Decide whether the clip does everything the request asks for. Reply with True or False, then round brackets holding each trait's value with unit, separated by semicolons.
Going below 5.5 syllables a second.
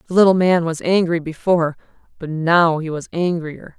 True (5.1 syllables/s)